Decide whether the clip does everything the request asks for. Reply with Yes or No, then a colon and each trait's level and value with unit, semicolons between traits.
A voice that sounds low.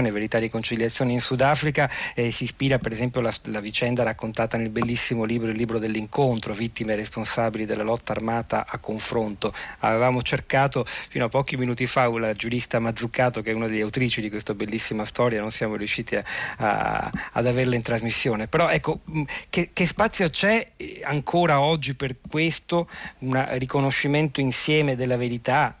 Yes: low, 120 Hz